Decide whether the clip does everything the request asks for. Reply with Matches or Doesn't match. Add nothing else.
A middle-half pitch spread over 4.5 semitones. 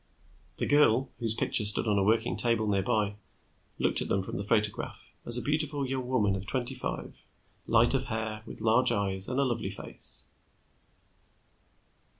Doesn't match